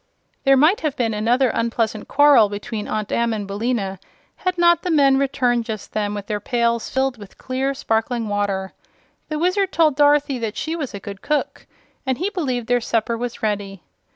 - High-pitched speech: Yes, high, 240 Hz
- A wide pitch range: No, average, 4.8 semitones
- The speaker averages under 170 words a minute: No, average, 185 wpm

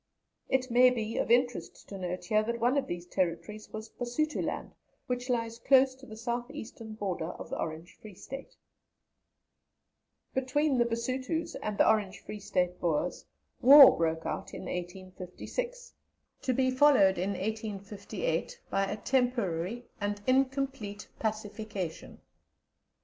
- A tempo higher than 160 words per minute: No, average, 140 wpm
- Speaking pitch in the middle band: No, high, 220 Hz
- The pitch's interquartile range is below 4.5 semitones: No, average, 4.8 semitones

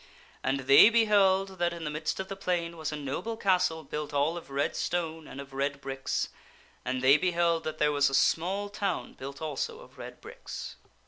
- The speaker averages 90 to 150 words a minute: No, average, 200 wpm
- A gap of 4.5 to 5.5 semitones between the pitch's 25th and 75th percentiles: Yes, average, 4.9 semitones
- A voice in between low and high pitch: Yes, medium, 160 Hz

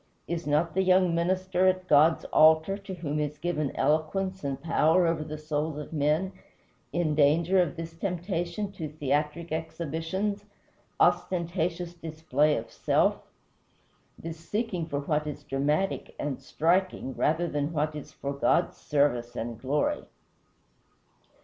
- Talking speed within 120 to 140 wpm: Yes, slow, 135 wpm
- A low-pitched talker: No, medium, 160 Hz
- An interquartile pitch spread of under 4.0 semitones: Yes, average, 2.8 semitones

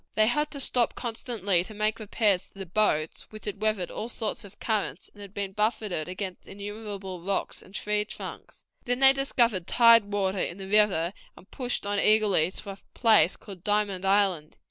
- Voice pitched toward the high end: Yes, high, 205 Hz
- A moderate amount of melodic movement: No, narrow, 2.3 semitones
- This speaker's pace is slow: No, average, 190 wpm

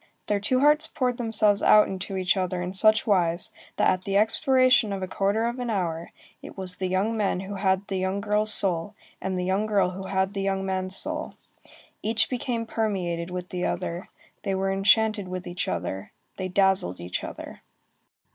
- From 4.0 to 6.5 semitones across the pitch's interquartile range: No, average, 2.7 semitones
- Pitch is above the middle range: Yes, high, 195 Hz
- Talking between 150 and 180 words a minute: No, average, 195 wpm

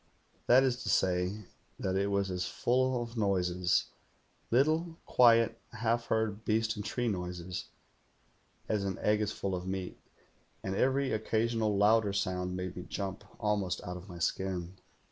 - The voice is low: Yes, low, 100 Hz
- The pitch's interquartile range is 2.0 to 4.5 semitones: Yes, average, 3.8 semitones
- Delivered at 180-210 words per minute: No, average, 165 wpm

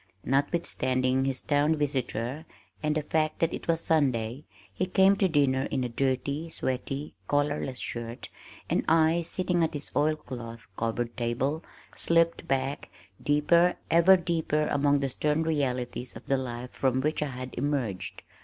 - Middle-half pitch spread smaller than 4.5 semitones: Yes, average, 3.7 semitones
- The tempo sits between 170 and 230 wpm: No, average, 155 wpm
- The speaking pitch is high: No, medium, 145 Hz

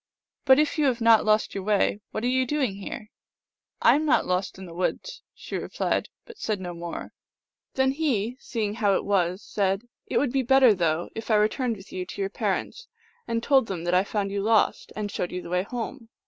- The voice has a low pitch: No, high, 215 Hz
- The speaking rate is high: Yes, fast, 230 wpm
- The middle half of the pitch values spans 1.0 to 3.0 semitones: No, average, 5.0 semitones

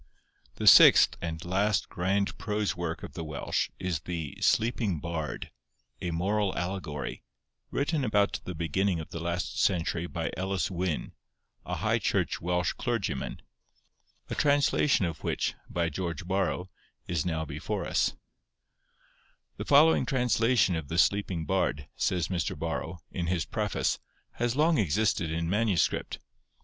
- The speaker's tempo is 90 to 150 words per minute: Yes, average, 140 wpm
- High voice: No, very low, 90 Hz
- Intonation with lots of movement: No, average, 3.8 semitones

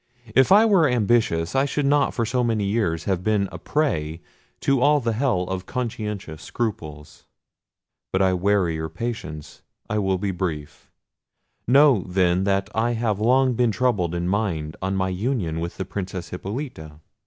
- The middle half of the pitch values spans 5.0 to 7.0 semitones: Yes, average, 5.3 semitones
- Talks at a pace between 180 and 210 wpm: No, average, 165 wpm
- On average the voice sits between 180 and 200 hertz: No, low, 100 Hz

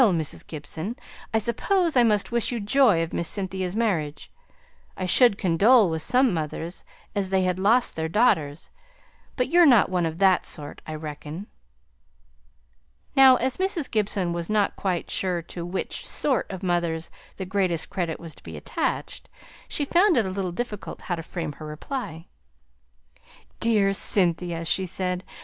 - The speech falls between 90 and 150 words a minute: No, average, 160 wpm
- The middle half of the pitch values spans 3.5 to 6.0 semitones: Yes, wide, 5.5 semitones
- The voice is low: No, high, 190 Hz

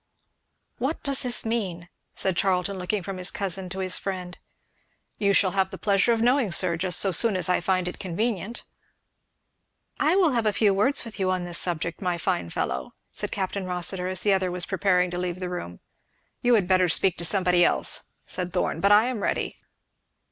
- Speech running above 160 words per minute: Yes, average, 200 wpm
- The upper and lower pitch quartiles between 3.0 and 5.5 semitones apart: No, narrow, 2.6 semitones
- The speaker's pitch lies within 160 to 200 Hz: Yes, medium, 185 Hz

